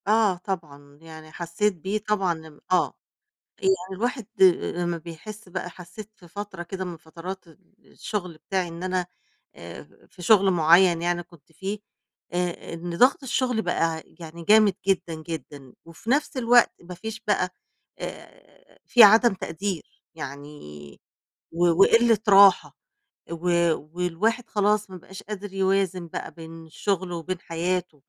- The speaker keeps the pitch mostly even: No, average, 3.7 semitones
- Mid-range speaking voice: Yes, medium, 180 Hz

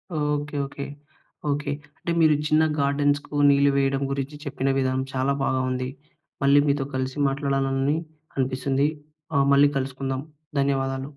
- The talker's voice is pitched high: No, medium, 140 Hz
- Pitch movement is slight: Yes, narrow, 1.2 semitones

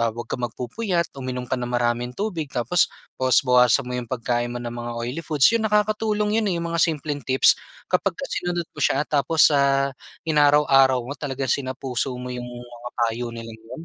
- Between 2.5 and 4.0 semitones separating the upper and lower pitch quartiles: No, average, 4.5 semitones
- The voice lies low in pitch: Yes, low, 130 Hz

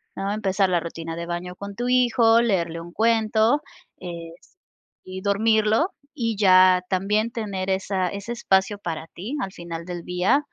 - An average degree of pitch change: Yes, average, 3.7 semitones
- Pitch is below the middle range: No, high, 195 Hz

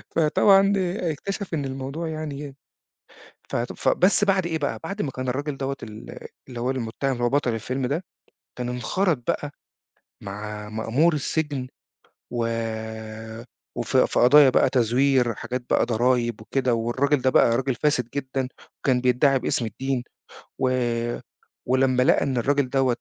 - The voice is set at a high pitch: No, low, 130 Hz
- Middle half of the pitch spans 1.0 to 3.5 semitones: Yes, average, 3.2 semitones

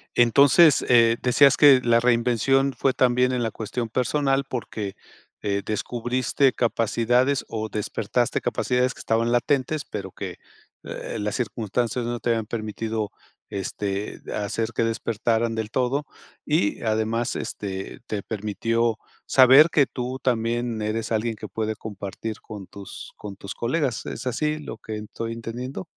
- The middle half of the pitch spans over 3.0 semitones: No, average, 2.7 semitones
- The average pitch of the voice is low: Yes, low, 115 Hz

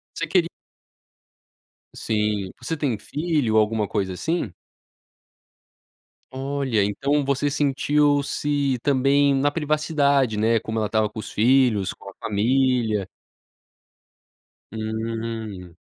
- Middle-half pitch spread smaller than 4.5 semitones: No, average, 4.8 semitones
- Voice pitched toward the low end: Yes, low, 125 Hz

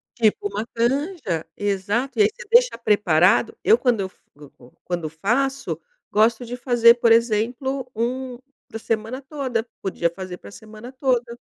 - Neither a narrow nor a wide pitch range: Yes, average, 4.0 semitones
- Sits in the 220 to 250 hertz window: Yes, high, 230 Hz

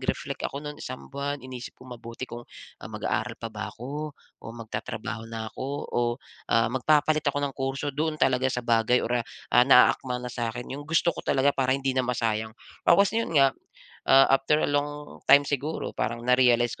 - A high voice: No, low, 130 Hz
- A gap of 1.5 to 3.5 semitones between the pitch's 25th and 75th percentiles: Yes, average, 2.9 semitones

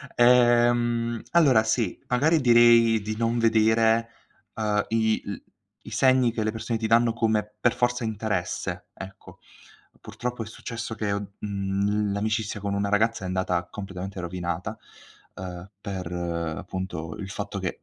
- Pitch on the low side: Yes, low, 110 Hz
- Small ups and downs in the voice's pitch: No, average, 3.0 semitones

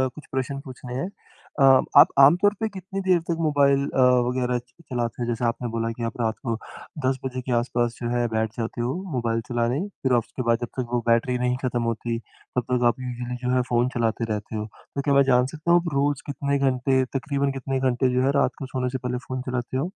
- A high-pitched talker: No, low, 125 Hz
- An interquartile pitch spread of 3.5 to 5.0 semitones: No, narrow, 2.4 semitones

